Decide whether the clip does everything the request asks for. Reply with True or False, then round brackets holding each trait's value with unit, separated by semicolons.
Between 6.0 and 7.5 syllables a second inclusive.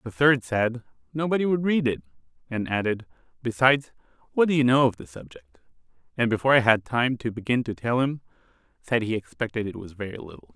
True (6.1 syllables/s)